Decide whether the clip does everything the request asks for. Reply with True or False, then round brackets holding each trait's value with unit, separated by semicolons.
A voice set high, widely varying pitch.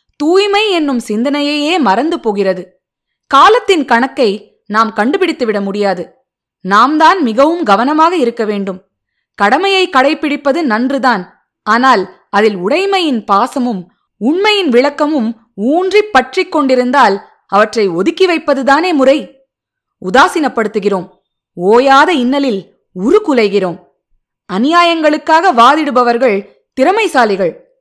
True (260 Hz; 7.0 semitones)